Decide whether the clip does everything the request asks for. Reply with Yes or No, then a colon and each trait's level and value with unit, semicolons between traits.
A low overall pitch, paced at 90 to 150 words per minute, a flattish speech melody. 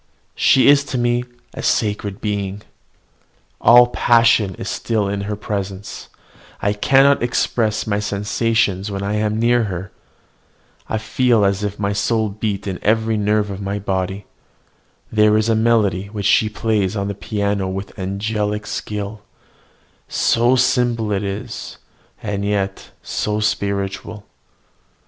Yes: low, 105 Hz; average, 140 wpm; narrow, 2.0 semitones